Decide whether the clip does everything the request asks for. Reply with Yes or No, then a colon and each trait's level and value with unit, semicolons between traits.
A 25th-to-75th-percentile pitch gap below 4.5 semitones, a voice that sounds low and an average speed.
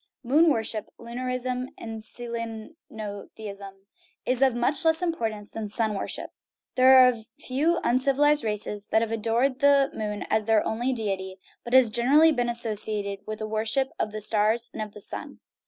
No: average, 3.2 semitones; high, 230 Hz; average, 170 wpm